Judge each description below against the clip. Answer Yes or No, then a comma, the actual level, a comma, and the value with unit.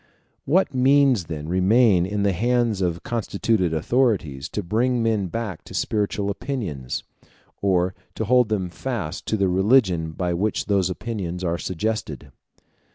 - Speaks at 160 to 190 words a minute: No, average, 145 wpm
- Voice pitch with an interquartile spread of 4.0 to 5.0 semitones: Yes, average, 4.7 semitones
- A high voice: No, low, 100 Hz